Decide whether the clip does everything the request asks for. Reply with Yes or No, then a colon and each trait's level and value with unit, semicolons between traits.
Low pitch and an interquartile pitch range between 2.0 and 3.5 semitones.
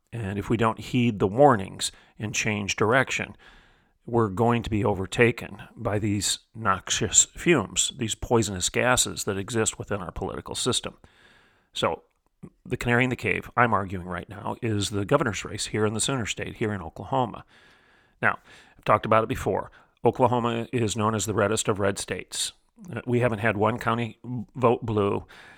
Yes: low, 110 Hz; average, 2.9 semitones